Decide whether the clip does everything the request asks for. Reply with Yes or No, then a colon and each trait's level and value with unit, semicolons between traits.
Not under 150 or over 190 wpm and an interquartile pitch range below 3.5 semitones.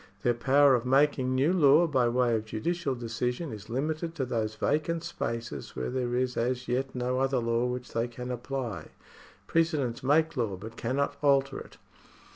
Yes: average, 175 wpm; average, 3.1 semitones